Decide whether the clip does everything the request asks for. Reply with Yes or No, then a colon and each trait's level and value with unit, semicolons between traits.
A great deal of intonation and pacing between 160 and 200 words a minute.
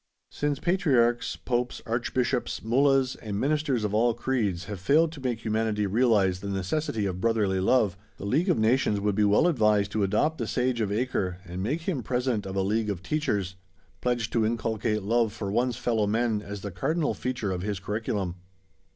No: average, 3.9 semitones; average, 185 wpm